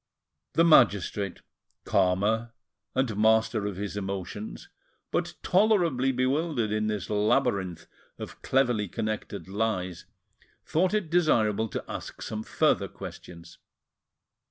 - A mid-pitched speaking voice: No, low, 110 Hz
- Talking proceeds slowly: Yes, slow, 110 wpm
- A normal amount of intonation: Yes, average, 4.6 semitones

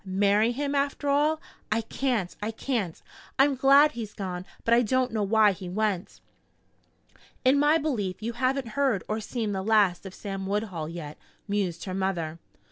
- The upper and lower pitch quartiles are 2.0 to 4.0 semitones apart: No, average, 5.2 semitones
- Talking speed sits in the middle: Yes, average, 170 wpm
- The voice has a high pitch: Yes, high, 215 Hz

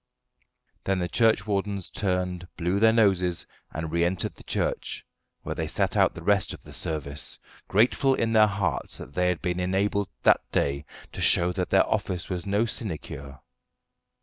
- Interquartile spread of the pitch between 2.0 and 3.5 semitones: Yes, average, 2.8 semitones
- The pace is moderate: Yes, average, 170 wpm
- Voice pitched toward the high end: No, very low, 95 Hz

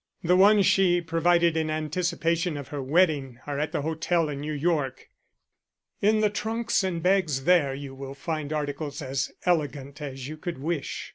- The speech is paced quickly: No, average, 170 wpm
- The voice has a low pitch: No, medium, 155 Hz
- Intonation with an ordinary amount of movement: Yes, average, 3.7 semitones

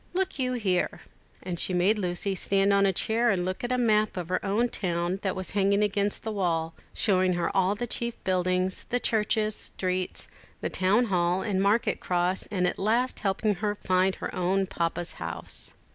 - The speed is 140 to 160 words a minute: No, average, 195 wpm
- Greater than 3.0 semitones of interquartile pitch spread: No, average, 2.7 semitones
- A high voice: Yes, high, 195 Hz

